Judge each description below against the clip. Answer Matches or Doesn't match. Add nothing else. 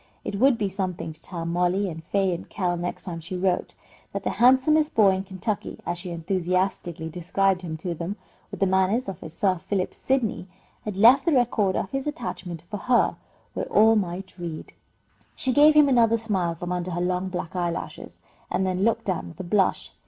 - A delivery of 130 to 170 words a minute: Doesn't match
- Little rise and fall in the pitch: Doesn't match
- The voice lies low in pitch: Doesn't match